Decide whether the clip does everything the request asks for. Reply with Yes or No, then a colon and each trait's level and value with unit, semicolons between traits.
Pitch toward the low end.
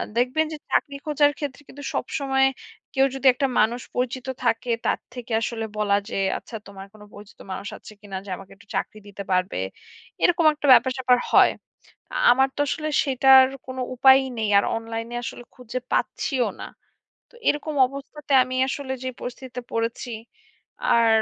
No: very high, 255 Hz